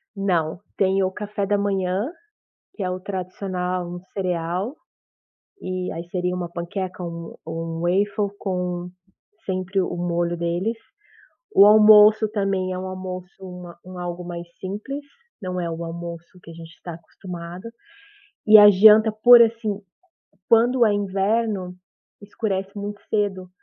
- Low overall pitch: No, medium, 185 Hz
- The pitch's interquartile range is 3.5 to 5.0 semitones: No, average, 2.7 semitones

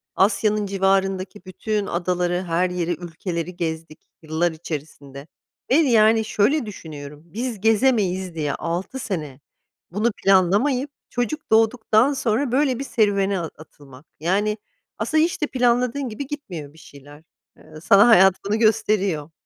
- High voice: Yes, high, 195 Hz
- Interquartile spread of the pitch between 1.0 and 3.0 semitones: No, average, 5.2 semitones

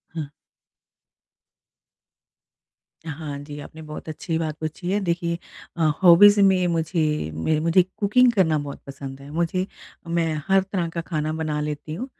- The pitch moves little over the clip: No, average, 3.1 semitones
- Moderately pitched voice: Yes, medium, 165 Hz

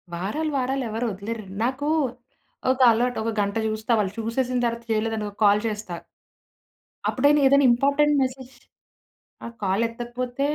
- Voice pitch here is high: Yes, high, 235 Hz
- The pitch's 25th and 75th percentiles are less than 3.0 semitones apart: No, average, 3.3 semitones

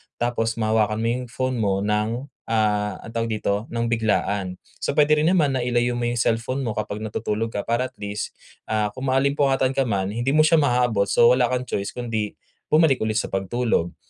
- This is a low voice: Yes, low, 115 Hz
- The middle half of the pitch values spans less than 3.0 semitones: No, average, 3.3 semitones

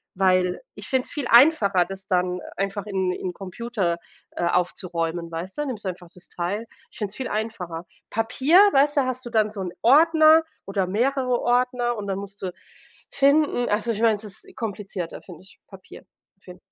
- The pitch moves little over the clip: No, average, 5.1 semitones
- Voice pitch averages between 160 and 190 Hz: No, high, 205 Hz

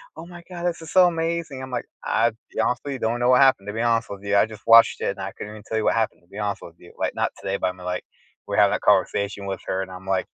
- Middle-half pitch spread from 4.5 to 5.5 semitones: Yes, average, 5.1 semitones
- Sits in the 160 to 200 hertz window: No, low, 110 Hz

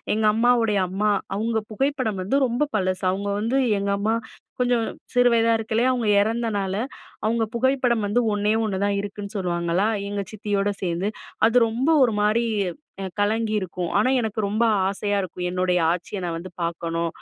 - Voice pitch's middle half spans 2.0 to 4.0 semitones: Yes, average, 3.1 semitones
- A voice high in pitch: Yes, high, 210 Hz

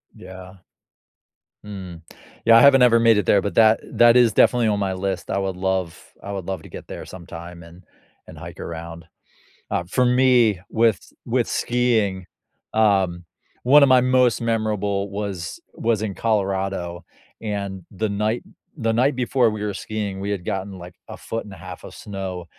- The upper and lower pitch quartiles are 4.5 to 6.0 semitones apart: No, average, 3.5 semitones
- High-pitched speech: No, low, 100 Hz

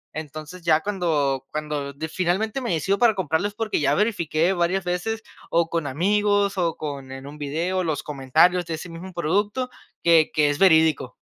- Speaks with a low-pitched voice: No, medium, 170 Hz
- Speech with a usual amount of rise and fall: Yes, average, 4.1 semitones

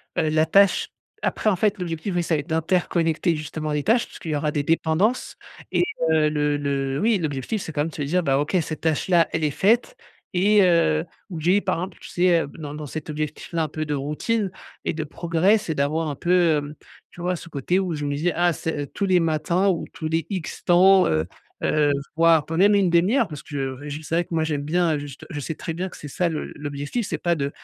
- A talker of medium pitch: Yes, medium, 160 Hz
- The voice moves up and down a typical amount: Yes, average, 3.2 semitones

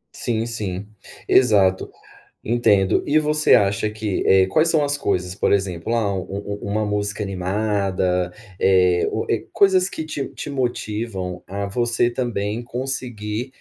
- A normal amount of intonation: Yes, average, 3.9 semitones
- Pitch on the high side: No, low, 105 Hz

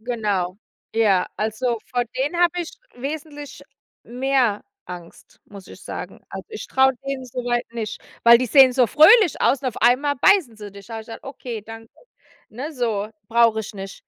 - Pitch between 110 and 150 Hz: No, high, 240 Hz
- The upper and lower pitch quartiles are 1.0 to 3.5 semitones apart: No, average, 4.0 semitones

